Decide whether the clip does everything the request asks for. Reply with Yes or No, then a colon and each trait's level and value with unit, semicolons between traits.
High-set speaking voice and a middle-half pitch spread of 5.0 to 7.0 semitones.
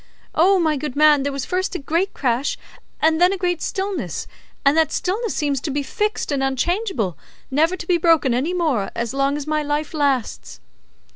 No: very high, 305 Hz; average, 4.5 semitones